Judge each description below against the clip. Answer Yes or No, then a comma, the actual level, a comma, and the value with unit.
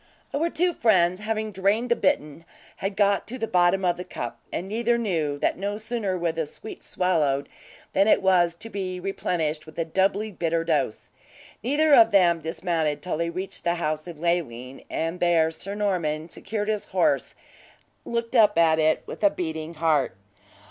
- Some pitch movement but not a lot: Yes, average, 4.3 semitones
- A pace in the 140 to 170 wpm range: No, average, 185 wpm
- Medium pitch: Yes, medium, 180 Hz